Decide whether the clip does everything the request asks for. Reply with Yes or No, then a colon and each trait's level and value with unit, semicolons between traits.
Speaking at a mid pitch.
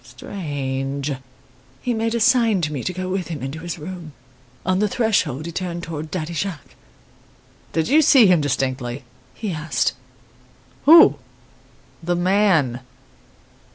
Yes: medium, 170 Hz